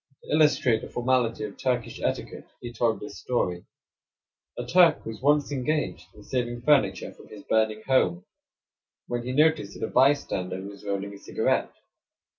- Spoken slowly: No, average, 160 wpm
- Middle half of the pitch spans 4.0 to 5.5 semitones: Yes, average, 4.7 semitones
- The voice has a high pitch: No, low, 120 Hz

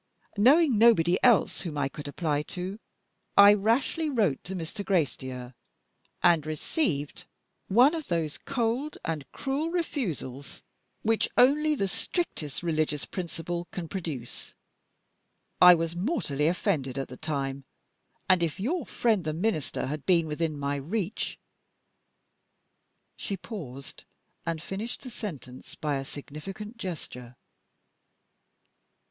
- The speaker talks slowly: Yes, slow, 125 wpm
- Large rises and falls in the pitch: Yes, wide, 6.9 semitones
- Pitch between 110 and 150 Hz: No, medium, 175 Hz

